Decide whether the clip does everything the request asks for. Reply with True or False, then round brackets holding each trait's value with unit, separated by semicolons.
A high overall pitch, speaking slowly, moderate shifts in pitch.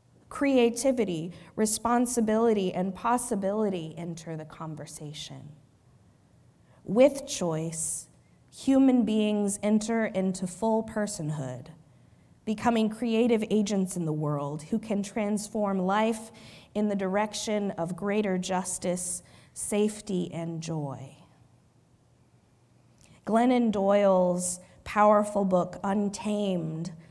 True (195 Hz; 85 wpm; 4.6 semitones)